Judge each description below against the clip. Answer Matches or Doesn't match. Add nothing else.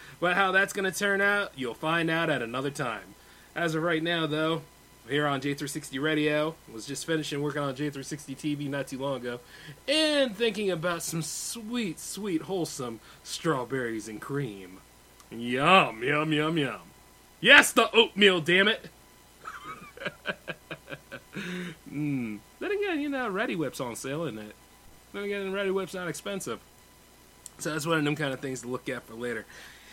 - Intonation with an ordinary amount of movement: Doesn't match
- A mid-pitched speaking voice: Matches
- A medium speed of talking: Matches